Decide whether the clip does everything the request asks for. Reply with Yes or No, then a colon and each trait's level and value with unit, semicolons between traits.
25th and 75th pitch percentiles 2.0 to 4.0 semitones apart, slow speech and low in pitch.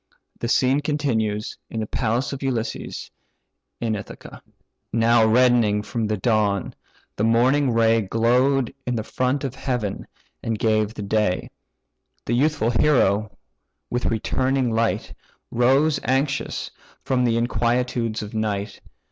Yes: average, 3.0 semitones; slow, 130 wpm; low, 115 Hz